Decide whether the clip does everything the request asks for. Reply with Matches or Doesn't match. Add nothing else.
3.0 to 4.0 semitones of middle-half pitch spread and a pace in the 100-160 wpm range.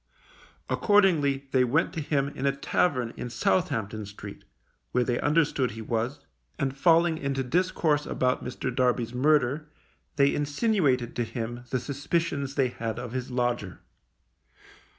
Matches